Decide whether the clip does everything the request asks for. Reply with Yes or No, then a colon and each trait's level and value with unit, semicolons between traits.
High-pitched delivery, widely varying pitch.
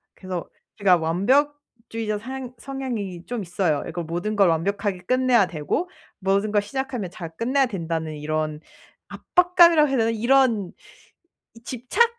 Yes: high, 215 Hz; wide, 6.7 semitones